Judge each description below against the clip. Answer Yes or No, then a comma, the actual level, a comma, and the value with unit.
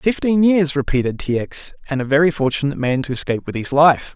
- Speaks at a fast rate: Yes, fast, 215 wpm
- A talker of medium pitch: Yes, medium, 145 Hz